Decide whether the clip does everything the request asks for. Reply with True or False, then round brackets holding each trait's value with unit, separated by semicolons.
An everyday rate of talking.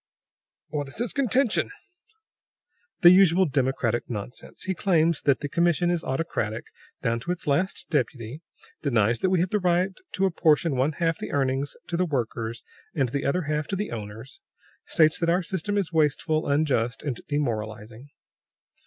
True (160 wpm)